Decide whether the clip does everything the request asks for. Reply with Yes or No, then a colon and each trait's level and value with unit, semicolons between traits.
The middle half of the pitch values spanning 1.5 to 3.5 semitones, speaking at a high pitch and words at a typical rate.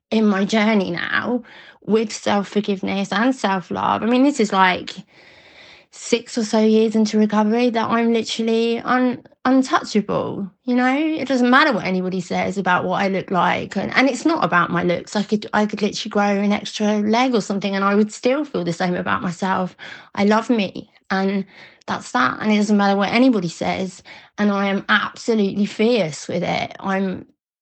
Yes: average, 3.2 semitones; high, 210 Hz; average, 185 wpm